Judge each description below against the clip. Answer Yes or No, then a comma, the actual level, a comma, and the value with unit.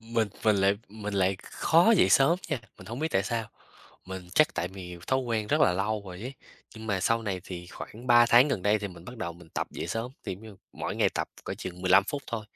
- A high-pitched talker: No, low, 105 Hz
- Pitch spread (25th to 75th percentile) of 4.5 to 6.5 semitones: No, average, 3.9 semitones